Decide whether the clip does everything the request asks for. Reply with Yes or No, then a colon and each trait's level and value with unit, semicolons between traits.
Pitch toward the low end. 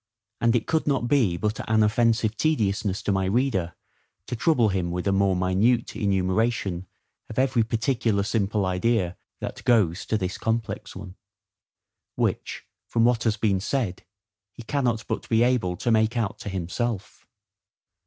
Yes: low, 110 Hz